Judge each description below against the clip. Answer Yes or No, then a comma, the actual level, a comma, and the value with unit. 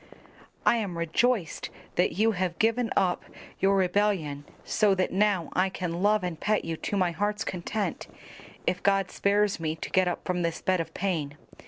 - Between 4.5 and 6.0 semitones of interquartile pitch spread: No, average, 3.2 semitones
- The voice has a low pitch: No, medium, 185 Hz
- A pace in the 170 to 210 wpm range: Yes, average, 180 wpm